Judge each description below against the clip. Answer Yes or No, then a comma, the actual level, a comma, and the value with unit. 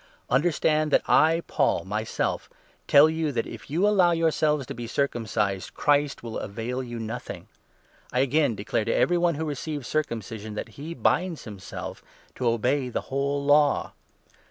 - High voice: No, medium, 140 Hz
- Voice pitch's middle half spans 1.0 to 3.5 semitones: No, average, 5.1 semitones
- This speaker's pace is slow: No, average, 165 wpm